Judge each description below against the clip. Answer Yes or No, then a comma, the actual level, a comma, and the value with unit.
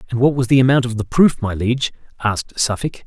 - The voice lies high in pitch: No, low, 120 Hz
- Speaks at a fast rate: Yes, fast, 235 wpm